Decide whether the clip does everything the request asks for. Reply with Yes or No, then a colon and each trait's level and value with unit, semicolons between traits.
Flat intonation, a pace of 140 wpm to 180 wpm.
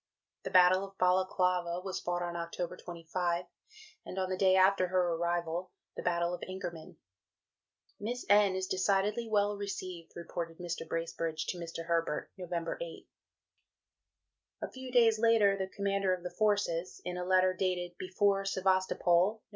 Yes: narrow, 2.3 semitones; average, 155 wpm